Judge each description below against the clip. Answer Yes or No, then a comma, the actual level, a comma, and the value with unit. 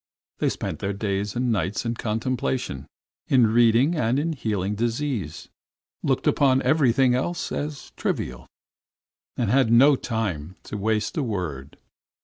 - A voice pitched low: Yes, low, 115 Hz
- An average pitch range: Yes, average, 4.6 semitones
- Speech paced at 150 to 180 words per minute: No, slow, 135 wpm